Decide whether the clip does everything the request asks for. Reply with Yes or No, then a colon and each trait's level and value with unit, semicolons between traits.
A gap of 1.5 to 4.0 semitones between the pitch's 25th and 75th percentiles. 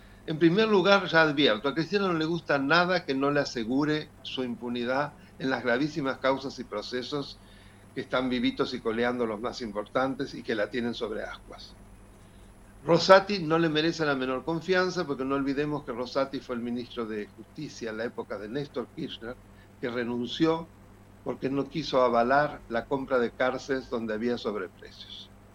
No: average, 4.6 semitones